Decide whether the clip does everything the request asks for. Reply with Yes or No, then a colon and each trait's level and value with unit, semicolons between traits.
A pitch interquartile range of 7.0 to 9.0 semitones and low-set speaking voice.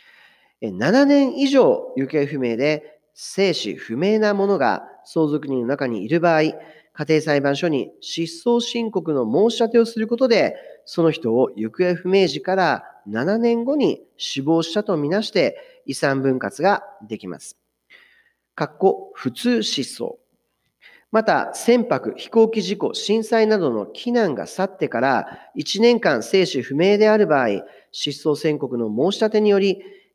No: wide, 7.6 semitones; high, 195 Hz